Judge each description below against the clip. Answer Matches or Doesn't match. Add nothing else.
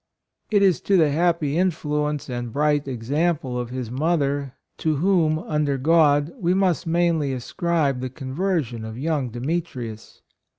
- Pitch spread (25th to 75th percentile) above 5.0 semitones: Doesn't match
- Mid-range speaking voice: Matches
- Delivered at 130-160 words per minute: Matches